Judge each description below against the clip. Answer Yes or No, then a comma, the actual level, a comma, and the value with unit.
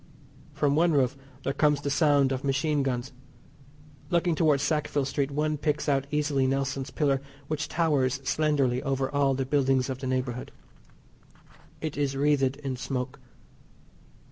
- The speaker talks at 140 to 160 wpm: Yes, average, 145 wpm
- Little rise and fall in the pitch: Yes, narrow, 1.9 semitones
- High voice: No, medium, 140 Hz